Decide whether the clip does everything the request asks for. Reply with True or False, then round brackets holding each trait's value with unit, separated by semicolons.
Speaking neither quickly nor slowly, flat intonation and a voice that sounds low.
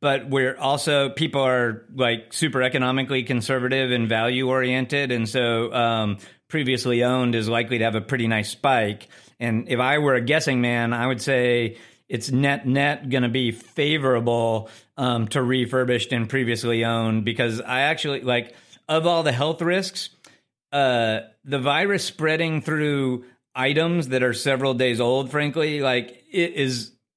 False (160 wpm; 3.0 semitones; 130 Hz)